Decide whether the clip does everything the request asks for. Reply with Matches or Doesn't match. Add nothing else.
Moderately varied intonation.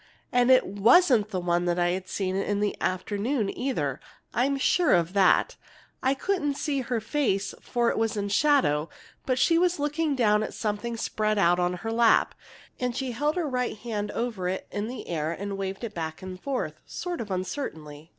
Doesn't match